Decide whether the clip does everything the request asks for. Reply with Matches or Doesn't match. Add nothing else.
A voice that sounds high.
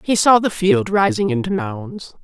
Matches